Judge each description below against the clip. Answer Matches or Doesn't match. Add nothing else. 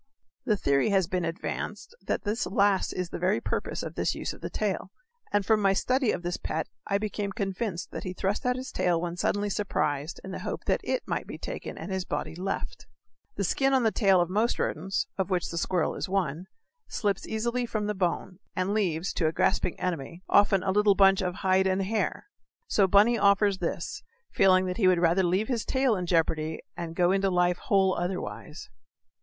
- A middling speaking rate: Doesn't match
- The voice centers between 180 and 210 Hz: Matches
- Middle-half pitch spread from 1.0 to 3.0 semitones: Matches